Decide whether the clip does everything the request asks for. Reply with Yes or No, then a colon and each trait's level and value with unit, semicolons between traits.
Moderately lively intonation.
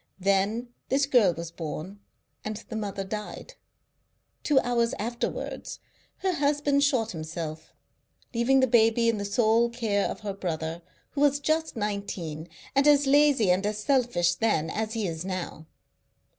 No: wide, 5.7 semitones